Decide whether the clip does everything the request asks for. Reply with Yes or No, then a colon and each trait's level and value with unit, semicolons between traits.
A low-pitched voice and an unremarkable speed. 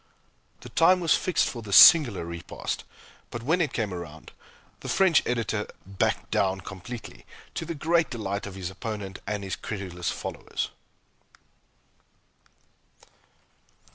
No: low, 105 Hz; slow, 130 wpm